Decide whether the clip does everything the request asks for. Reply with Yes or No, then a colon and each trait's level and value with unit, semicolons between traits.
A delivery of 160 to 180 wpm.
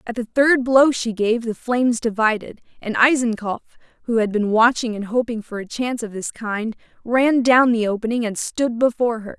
No: average, 200 wpm